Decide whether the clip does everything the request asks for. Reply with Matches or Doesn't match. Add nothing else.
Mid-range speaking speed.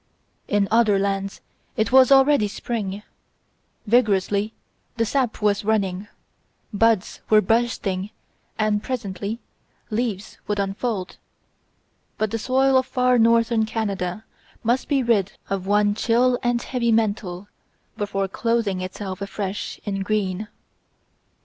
Doesn't match